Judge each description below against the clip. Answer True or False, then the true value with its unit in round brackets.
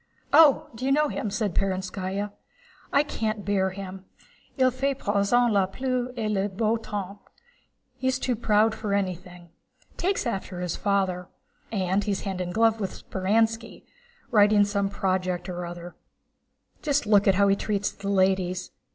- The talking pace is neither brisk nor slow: True (155 wpm)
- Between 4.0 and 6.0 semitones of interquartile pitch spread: False (3.1 semitones)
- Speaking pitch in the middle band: False (200 Hz)